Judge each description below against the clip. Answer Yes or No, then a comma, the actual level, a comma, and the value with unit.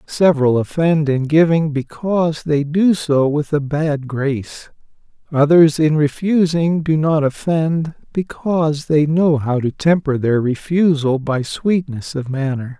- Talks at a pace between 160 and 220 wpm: No, average, 140 wpm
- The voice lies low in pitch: No, medium, 150 Hz